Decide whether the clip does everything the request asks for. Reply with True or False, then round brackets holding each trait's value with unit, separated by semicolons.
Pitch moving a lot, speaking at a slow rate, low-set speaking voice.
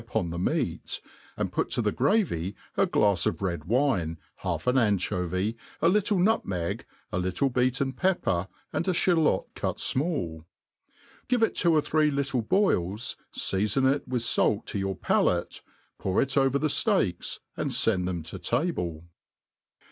False (8.5 semitones; 155 wpm; 120 Hz)